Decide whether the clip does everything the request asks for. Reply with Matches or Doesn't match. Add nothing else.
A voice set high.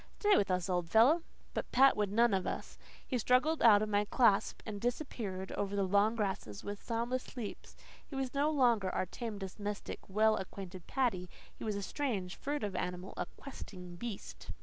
Matches